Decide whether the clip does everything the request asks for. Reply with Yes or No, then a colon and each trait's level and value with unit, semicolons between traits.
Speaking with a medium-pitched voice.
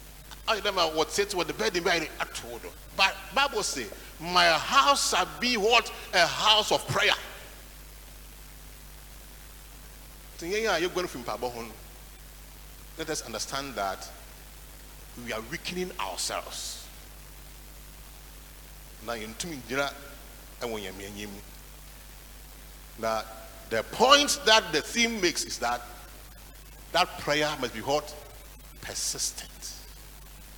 Yes: medium, 155 Hz